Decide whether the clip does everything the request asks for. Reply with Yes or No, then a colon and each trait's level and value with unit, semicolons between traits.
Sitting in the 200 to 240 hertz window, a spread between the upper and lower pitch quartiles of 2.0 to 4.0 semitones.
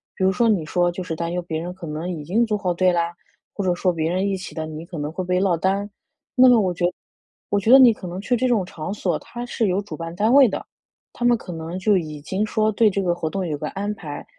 No: medium, 185 Hz; average, 3.5 semitones